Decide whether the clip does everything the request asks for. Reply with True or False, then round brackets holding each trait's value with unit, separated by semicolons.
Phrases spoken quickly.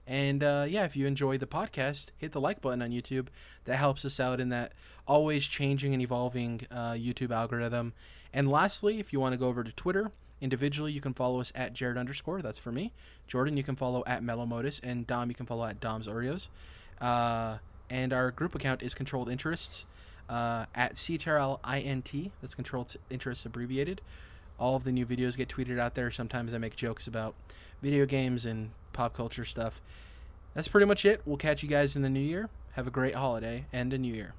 True (215 wpm)